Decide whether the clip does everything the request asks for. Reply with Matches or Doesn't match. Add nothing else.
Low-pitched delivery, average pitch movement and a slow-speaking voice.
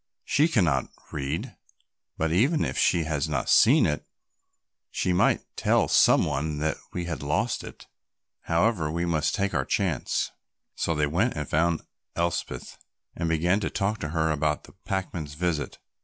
Doesn't match